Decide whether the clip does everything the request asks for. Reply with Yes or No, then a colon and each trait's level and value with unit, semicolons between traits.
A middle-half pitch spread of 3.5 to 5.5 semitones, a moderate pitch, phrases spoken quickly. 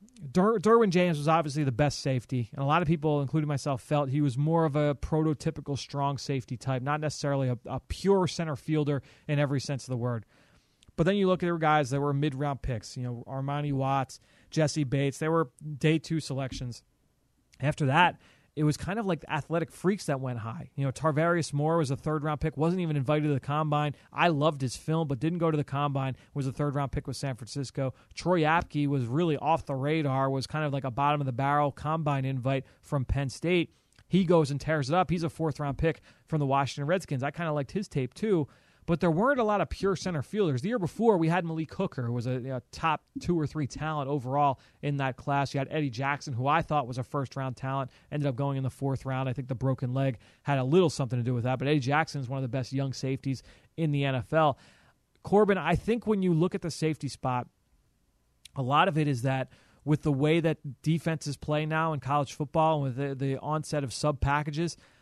No: average, 2.9 semitones; medium, 145 Hz; fast, 240 wpm